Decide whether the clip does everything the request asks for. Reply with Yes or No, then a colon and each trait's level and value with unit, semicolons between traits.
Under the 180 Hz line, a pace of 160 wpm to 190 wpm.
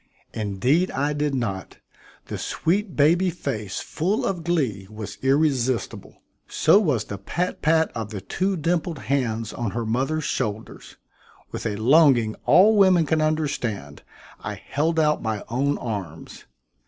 No: medium, 140 Hz; average, 140 wpm